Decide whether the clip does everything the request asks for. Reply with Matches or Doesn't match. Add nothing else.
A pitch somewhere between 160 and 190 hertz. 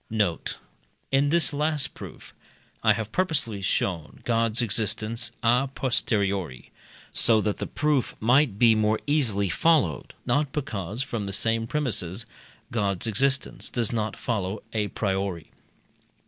Doesn't match